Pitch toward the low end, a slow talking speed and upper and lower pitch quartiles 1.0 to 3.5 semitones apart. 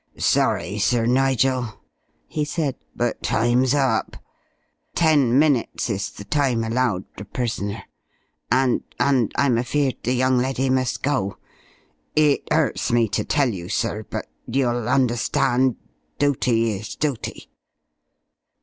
Yes: low, 125 Hz; slow, 120 wpm; average, 2.8 semitones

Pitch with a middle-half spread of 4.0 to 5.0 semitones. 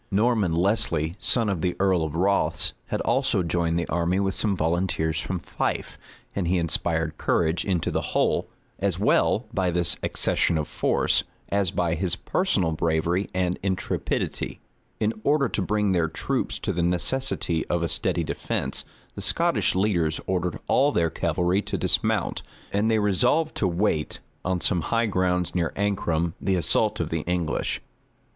No: average, 3.1 semitones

